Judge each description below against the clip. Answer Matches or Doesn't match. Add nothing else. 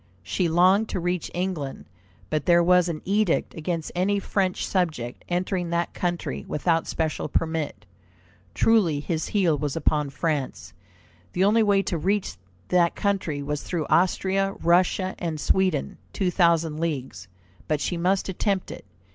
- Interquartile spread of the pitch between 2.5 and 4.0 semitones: Matches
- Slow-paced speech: Doesn't match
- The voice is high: Doesn't match